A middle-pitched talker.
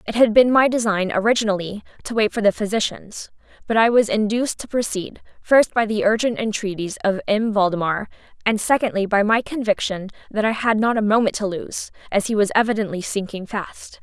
No: high, 215 Hz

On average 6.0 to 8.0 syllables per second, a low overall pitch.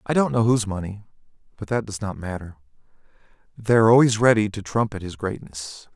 Yes: 6.1 syllables/s; low, 105 Hz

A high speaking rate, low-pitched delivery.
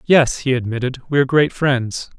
No: average, 165 wpm; low, 130 Hz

